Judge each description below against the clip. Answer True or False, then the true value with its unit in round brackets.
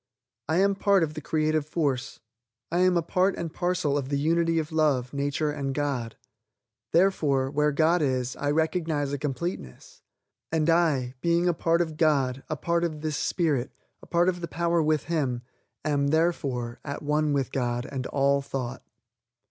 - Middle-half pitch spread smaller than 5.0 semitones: True (3.3 semitones)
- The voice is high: False (150 Hz)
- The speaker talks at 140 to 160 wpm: False (175 wpm)